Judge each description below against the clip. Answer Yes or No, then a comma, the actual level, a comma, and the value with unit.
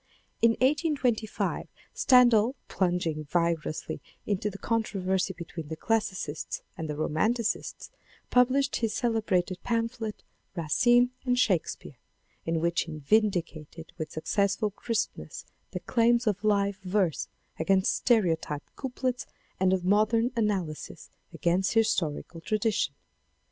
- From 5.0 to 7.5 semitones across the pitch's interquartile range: Yes, average, 5.3 semitones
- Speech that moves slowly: Yes, slow, 115 wpm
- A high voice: Yes, high, 200 Hz